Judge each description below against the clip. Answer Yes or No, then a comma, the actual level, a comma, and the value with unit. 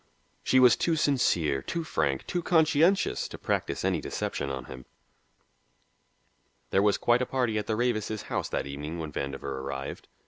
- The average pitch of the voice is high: No, low, 105 Hz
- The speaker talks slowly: No, average, 165 wpm